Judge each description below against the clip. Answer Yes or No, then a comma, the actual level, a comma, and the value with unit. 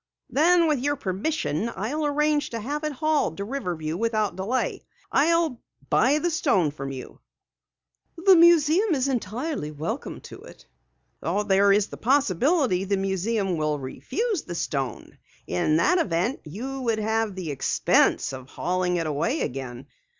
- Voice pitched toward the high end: Yes, high, 220 Hz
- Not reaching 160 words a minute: Yes, average, 150 wpm